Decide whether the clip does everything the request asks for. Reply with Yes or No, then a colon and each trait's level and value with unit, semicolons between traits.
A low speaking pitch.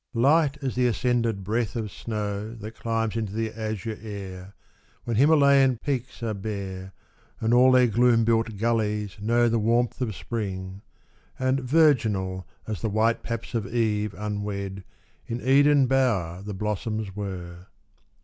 Yes: low, 110 Hz